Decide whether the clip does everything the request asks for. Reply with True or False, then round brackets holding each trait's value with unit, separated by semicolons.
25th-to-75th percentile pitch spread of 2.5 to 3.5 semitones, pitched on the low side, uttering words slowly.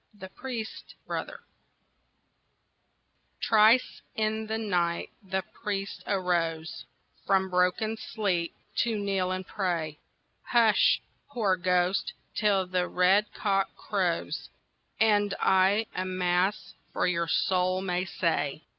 False (2.8 semitones; 190 Hz; 110 wpm)